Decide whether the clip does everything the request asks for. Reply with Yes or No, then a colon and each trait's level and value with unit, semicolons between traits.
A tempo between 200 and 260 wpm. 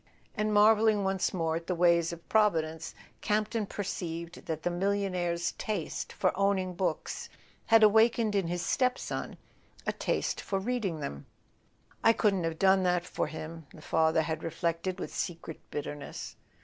No: average, 155 wpm